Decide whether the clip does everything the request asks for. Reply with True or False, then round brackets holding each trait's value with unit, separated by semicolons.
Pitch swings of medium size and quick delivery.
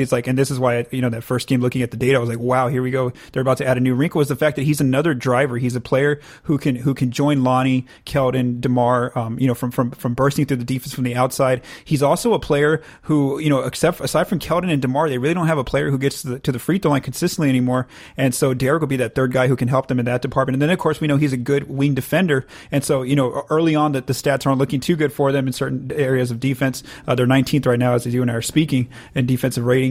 False (2.2 semitones; 300 wpm)